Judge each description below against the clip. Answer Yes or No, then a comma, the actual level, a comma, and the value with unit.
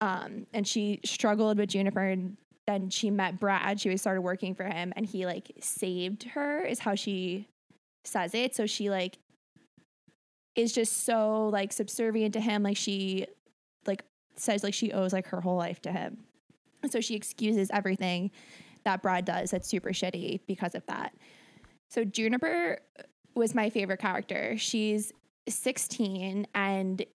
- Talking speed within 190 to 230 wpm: No, average, 155 wpm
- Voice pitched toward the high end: Yes, high, 205 Hz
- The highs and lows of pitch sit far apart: No, average, 2.7 semitones